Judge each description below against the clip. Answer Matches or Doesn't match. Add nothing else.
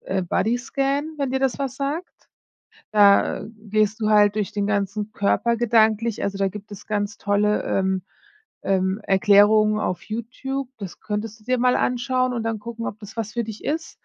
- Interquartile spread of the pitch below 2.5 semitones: Doesn't match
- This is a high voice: Matches